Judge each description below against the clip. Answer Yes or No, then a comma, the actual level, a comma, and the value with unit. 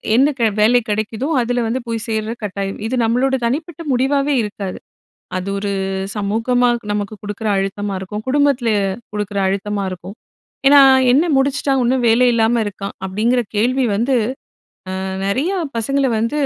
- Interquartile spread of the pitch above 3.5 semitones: Yes, average, 4.0 semitones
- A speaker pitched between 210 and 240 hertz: Yes, high, 230 Hz